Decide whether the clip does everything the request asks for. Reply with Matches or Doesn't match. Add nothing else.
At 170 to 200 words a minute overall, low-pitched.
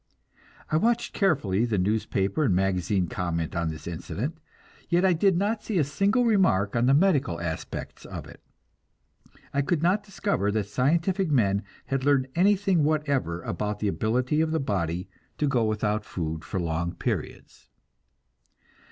Doesn't match